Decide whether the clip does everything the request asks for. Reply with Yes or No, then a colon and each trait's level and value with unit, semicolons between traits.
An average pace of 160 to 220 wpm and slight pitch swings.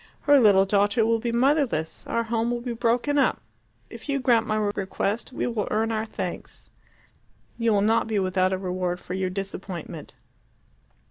No: average, 180 wpm; average, 3.6 semitones